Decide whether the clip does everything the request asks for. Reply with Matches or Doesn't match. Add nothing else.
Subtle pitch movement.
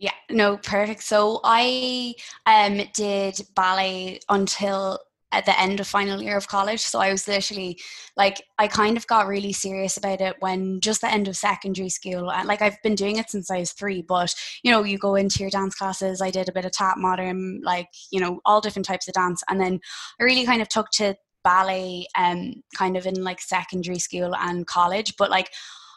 Matches